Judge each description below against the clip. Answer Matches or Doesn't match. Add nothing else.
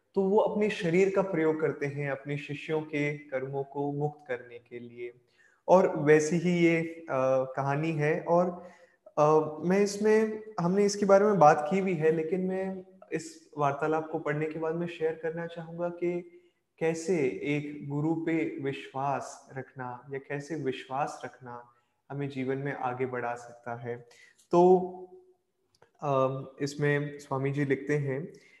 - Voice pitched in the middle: Matches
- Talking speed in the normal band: Matches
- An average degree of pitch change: Matches